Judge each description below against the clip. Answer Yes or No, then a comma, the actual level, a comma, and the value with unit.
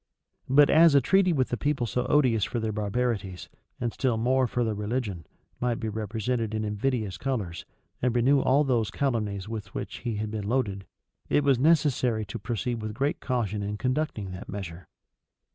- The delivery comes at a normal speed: Yes, average, 180 wpm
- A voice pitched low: Yes, low, 115 Hz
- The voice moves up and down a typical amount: Yes, average, 3.8 semitones